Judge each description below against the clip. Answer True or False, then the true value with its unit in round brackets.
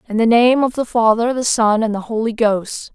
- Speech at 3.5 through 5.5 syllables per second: True (5.1 syllables/s)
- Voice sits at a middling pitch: False (225 Hz)